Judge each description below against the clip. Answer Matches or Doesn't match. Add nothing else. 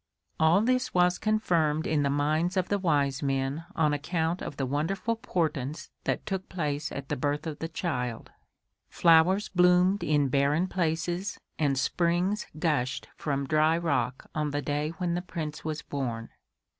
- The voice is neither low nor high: Matches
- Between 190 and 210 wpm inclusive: Doesn't match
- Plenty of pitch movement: Doesn't match